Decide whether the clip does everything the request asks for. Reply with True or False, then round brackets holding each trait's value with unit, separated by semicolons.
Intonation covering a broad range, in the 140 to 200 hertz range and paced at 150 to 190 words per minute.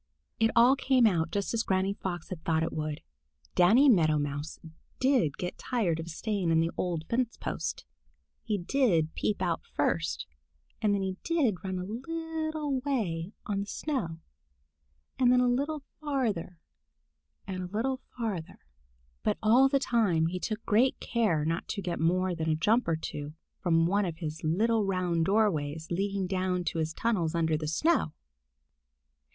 True (6.2 semitones; 190 Hz; 170 wpm)